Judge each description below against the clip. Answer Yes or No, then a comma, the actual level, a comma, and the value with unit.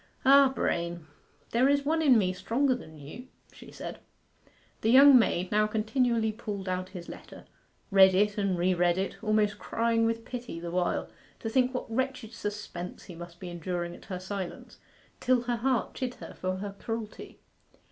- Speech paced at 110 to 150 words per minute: No, average, 175 wpm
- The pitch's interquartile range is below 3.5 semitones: No, average, 5.0 semitones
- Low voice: No, high, 210 Hz